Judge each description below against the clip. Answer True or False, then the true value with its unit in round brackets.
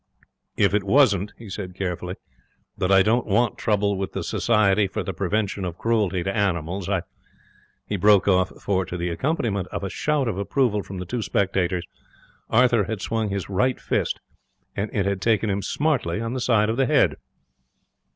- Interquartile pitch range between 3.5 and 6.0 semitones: False (3.0 semitones)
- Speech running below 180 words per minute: False (190 wpm)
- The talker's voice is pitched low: True (100 Hz)